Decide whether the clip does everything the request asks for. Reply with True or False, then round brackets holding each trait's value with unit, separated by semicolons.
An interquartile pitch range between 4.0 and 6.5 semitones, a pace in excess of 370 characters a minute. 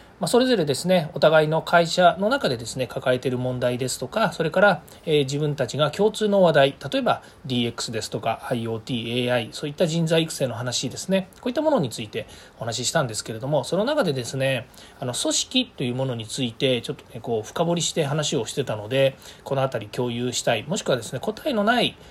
True (5.6 semitones; 430 characters per minute)